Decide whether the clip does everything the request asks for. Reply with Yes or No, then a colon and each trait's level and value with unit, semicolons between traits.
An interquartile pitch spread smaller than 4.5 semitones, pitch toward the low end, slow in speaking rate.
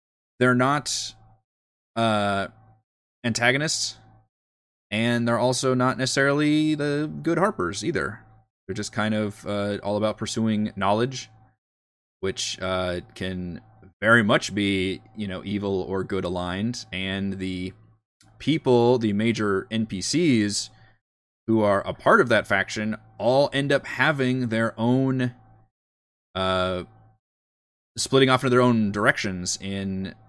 Yes: average, 3.9 semitones; low, 110 Hz; slow, 120 wpm